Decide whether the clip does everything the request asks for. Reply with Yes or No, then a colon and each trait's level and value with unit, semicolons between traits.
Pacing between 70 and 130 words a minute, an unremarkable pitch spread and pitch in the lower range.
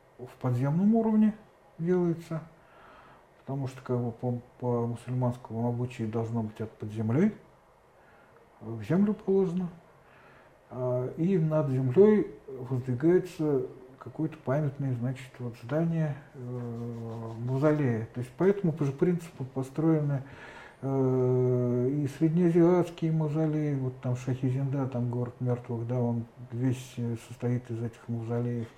Yes: average, 115 wpm; average, 4.6 semitones; low, 130 Hz